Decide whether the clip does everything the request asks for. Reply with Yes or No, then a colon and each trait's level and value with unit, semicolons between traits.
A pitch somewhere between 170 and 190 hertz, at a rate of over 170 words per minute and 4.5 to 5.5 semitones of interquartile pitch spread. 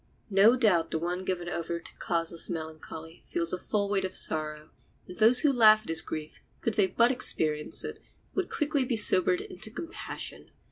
Yes: medium, 185 Hz; average, 185 wpm; average, 5.1 semitones